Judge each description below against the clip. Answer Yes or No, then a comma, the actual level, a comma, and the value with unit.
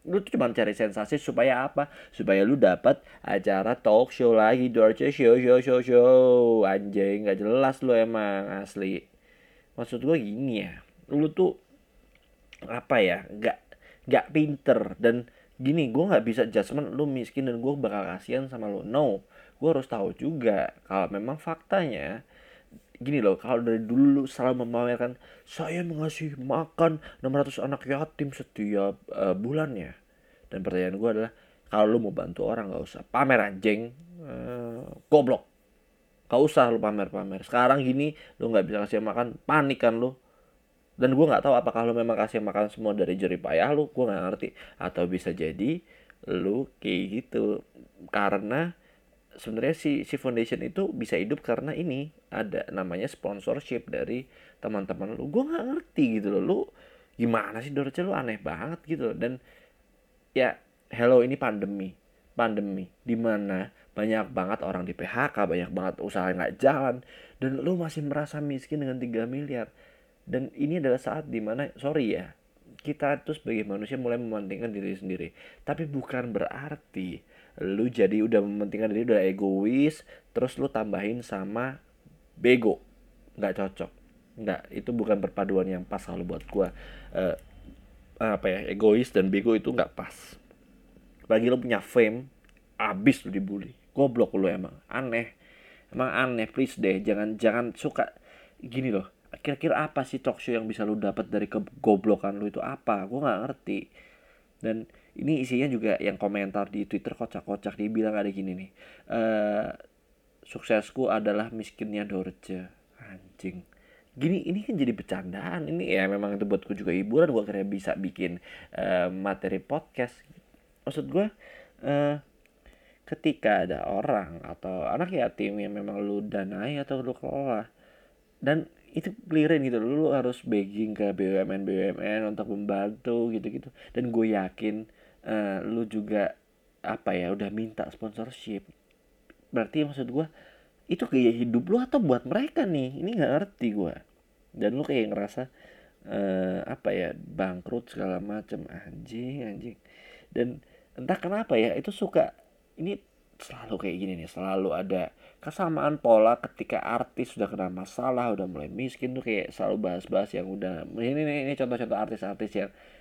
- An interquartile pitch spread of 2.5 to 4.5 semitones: No, wide, 5.4 semitones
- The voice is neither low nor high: No, low, 115 Hz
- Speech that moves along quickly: Yes, fast, 150 wpm